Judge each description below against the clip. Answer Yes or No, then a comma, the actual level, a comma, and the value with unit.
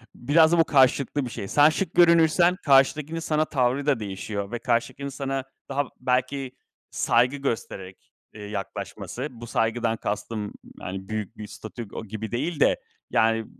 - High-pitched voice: No, low, 125 Hz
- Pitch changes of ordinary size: Yes, average, 4.7 semitones